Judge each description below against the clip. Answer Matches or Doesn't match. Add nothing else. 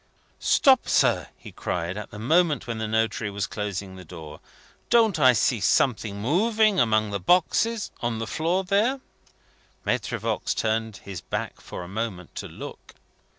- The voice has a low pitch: Matches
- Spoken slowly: Doesn't match